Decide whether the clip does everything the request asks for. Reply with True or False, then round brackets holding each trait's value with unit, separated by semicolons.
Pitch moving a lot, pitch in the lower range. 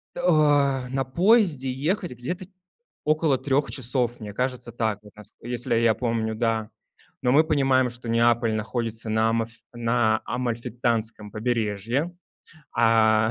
False (3.0 semitones; 120 Hz)